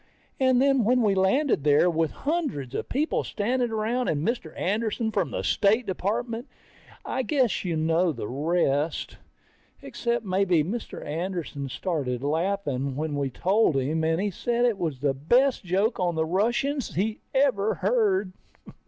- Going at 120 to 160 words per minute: Yes, average, 155 wpm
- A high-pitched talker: Yes, high, 195 Hz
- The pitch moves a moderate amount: No, wide, 6.9 semitones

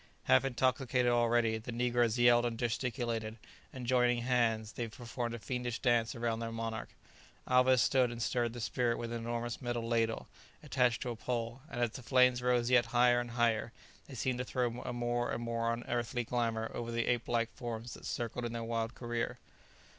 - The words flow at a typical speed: Yes, average, 190 wpm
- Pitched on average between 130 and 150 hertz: No, low, 120 Hz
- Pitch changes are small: Yes, narrow, 1.0 semitones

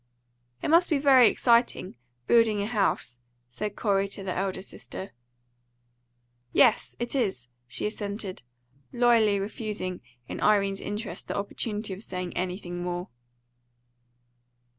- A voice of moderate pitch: No, high, 205 Hz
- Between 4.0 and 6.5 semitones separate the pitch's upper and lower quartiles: No, average, 3.3 semitones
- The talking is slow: Yes, slow, 120 wpm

